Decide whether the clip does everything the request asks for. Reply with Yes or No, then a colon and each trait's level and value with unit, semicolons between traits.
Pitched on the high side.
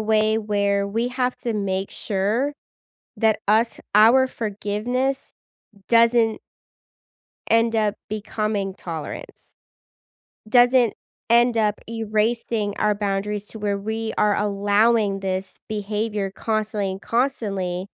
Yes: high, 215 Hz